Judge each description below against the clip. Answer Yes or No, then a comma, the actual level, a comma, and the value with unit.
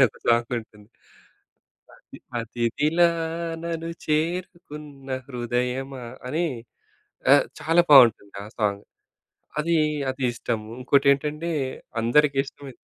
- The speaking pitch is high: No, low, 135 Hz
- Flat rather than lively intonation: No, average, 4.3 semitones